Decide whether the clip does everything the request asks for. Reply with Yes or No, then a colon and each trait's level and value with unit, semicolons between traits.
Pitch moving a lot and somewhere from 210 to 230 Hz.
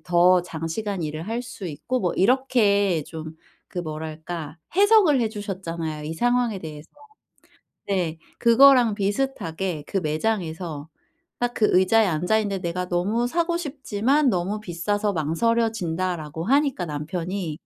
No: wide, 5.9 semitones; high, 190 Hz